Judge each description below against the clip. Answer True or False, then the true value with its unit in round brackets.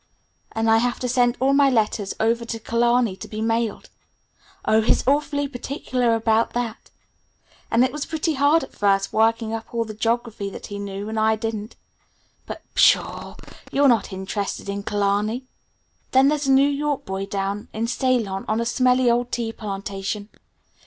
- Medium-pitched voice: False (230 Hz)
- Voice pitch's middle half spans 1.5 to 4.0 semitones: True (3.3 semitones)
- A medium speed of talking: True (175 wpm)